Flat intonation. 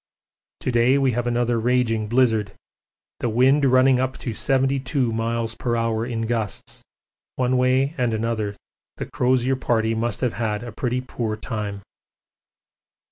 Yes: narrow, 2.2 semitones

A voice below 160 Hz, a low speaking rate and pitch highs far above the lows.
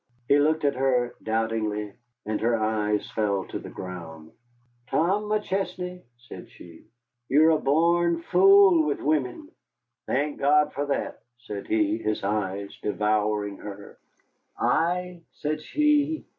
Yes: low, 135 Hz; slow, 130 wpm; wide, 8.0 semitones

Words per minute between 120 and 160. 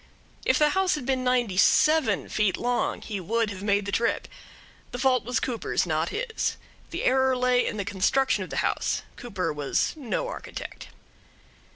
No: average, 175 wpm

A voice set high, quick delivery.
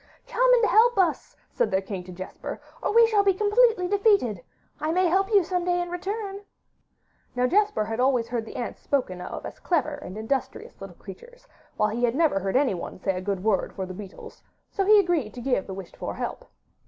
Yes: very high, 305 Hz; fast, 210 wpm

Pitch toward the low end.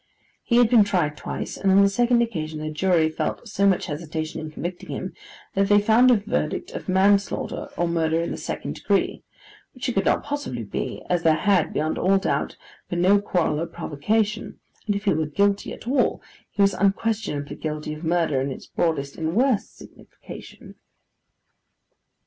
No: medium, 185 Hz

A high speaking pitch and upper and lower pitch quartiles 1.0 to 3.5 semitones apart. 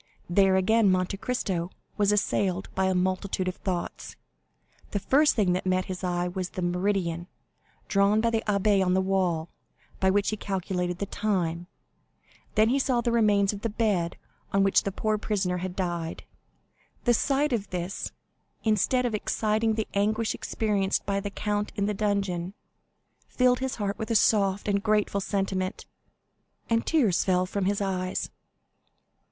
Yes: high, 200 Hz; narrow, 2.6 semitones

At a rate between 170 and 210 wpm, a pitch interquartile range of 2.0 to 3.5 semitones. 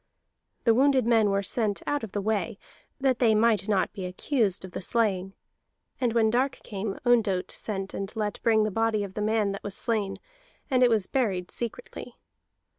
Yes: average, 190 wpm; average, 2.9 semitones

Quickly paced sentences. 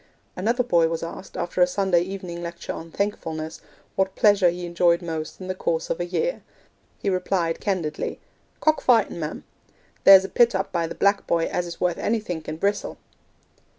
No: average, 185 wpm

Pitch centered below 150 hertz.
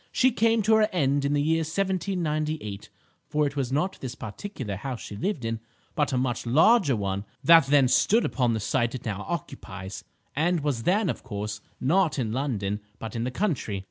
Yes: medium, 140 Hz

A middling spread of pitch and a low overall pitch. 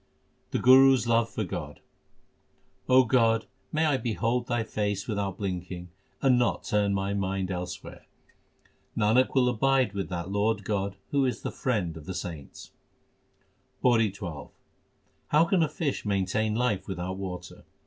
Yes: average, 4.6 semitones; low, 105 Hz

